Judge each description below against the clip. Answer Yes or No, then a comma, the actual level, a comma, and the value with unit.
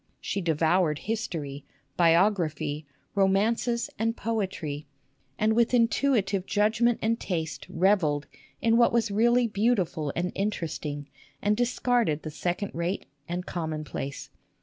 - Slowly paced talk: Yes, slow, 120 wpm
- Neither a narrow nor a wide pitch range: No, wide, 6.1 semitones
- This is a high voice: Yes, high, 195 Hz